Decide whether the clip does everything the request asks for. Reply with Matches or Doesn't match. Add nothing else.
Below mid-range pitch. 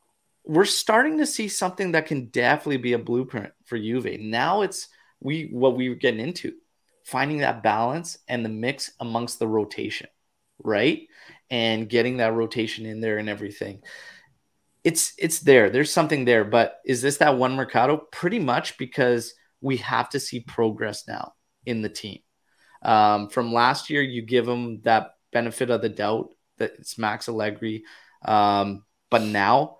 Matches